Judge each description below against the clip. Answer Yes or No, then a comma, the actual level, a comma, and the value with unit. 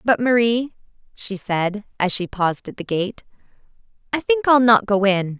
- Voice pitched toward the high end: Yes, high, 210 Hz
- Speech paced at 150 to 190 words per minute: Yes, average, 180 wpm